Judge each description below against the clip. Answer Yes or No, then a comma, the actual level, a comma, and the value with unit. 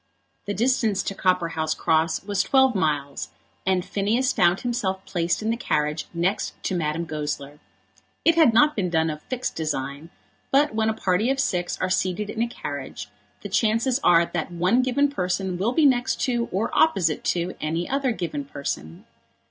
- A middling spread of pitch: No, wide, 6.2 semitones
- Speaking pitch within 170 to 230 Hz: Yes, high, 190 Hz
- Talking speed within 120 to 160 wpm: No, average, 175 wpm